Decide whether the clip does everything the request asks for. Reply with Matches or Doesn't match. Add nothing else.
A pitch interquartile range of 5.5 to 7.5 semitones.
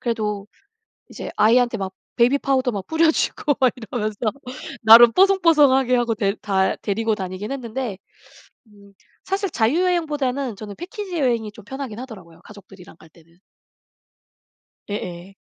Doesn't match